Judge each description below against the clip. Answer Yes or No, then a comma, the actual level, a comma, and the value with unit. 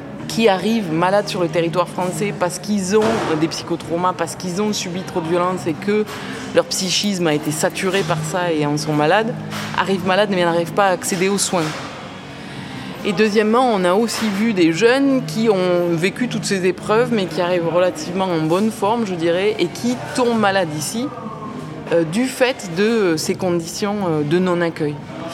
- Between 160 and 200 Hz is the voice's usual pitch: Yes, medium, 185 Hz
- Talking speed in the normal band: Yes, average, 180 wpm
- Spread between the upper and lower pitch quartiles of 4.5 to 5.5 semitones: No, average, 3.8 semitones